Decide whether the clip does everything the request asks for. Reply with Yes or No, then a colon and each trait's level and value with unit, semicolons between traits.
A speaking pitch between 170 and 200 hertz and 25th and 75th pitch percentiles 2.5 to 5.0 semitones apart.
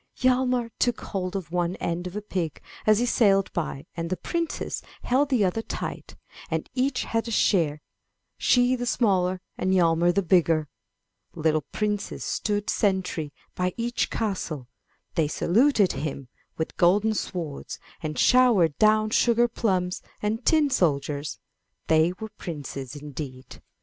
No: high, 190 Hz; wide, 5.6 semitones